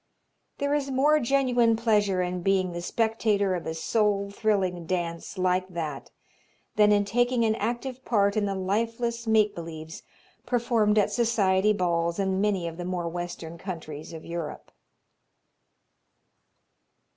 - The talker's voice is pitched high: Yes, high, 200 Hz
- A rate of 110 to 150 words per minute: Yes, average, 140 wpm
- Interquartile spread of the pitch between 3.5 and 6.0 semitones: Yes, average, 4.5 semitones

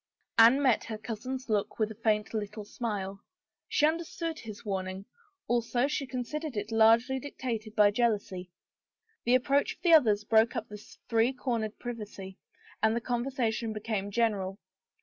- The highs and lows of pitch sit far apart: No, average, 3.2 semitones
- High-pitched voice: Yes, high, 225 Hz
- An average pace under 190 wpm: Yes, average, 155 wpm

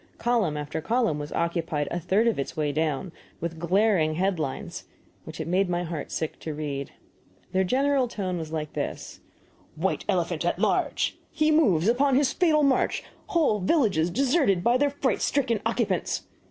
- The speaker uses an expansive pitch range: Yes, wide, 8.0 semitones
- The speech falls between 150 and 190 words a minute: Yes, average, 175 wpm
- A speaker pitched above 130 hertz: Yes, medium, 185 Hz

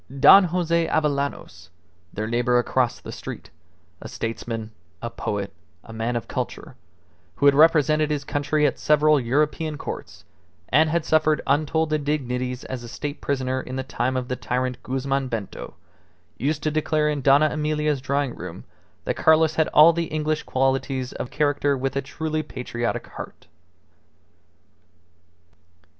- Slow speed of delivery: No, average, 150 wpm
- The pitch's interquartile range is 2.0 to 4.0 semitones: Yes, average, 3.3 semitones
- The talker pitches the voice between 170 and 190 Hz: No, medium, 140 Hz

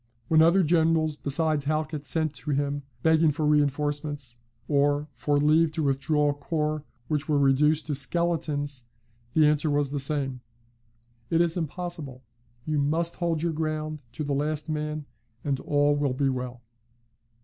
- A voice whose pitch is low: No, medium, 150 Hz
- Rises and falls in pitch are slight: Yes, narrow, 1.8 semitones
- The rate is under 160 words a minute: Yes, average, 150 wpm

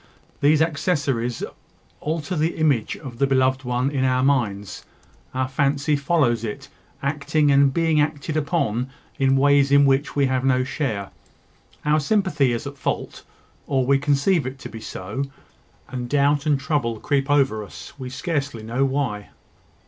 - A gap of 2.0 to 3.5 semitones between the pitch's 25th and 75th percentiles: Yes, narrow, 2.4 semitones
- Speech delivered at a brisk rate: No, average, 155 wpm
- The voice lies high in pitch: No, medium, 140 Hz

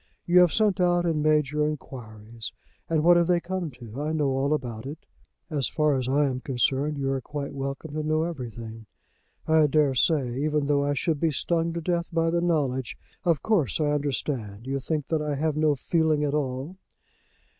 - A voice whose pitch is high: No, medium, 150 Hz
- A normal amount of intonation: Yes, average, 3.2 semitones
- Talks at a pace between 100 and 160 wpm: No, average, 200 wpm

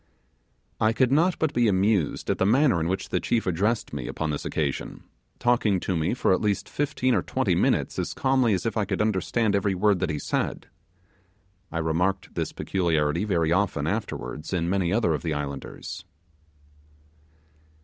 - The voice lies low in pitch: Yes, very low, 95 Hz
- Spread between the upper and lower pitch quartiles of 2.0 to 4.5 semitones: No, average, 5.3 semitones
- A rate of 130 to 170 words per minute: No, average, 180 wpm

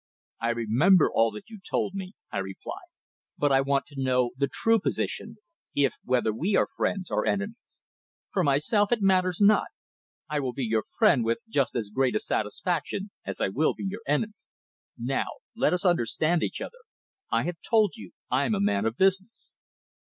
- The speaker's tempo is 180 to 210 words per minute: Yes, average, 185 wpm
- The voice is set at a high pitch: No, medium, 155 Hz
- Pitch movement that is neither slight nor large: No, wide, 7.9 semitones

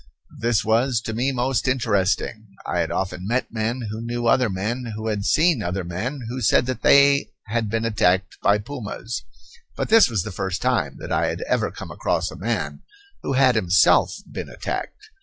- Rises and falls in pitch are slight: No, average, 3.8 semitones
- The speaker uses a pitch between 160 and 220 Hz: No, low, 115 Hz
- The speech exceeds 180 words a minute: Yes, average, 190 wpm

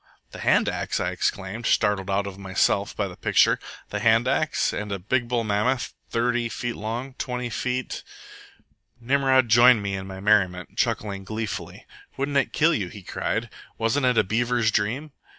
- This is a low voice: Yes, low, 115 Hz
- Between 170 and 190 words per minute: Yes, average, 175 wpm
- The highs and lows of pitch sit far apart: No, average, 3.7 semitones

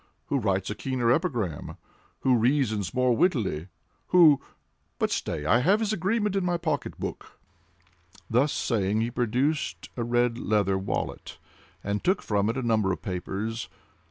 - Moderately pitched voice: No, low, 120 Hz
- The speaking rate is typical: Yes, average, 150 wpm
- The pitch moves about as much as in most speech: No, wide, 6.1 semitones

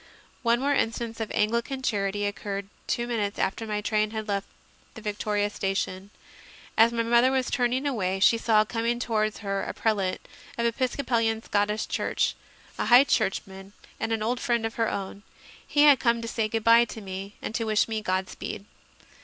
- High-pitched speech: Yes, high, 220 Hz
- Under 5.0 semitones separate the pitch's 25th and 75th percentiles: Yes, narrow, 2.4 semitones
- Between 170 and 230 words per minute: Yes, average, 185 wpm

